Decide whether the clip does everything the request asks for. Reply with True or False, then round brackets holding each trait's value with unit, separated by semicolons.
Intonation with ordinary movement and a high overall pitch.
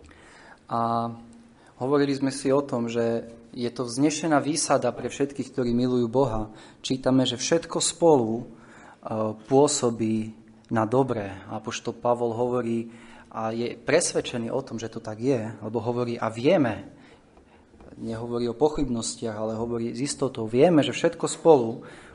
False (3.0 semitones; 120 Hz)